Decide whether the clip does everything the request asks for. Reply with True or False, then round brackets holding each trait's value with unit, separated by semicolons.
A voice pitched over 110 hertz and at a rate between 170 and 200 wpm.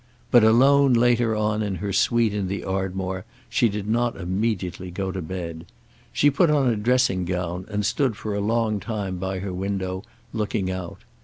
False (100 Hz; 180 wpm)